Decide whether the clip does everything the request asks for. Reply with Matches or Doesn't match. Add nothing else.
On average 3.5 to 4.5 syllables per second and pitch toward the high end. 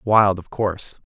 Doesn't match